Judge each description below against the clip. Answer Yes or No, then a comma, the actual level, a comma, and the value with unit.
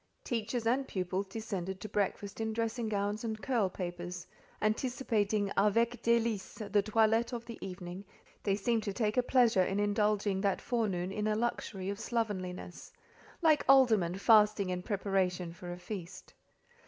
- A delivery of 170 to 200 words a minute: No, average, 155 wpm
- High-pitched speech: Yes, high, 210 Hz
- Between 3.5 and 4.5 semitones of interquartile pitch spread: No, average, 3.1 semitones